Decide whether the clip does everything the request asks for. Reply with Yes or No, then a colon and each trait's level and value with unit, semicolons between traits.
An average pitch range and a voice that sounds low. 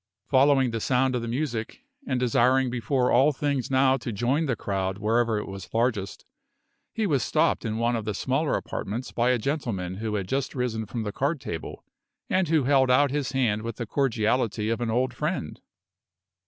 Yes: average, 3.2 semitones; low, 120 Hz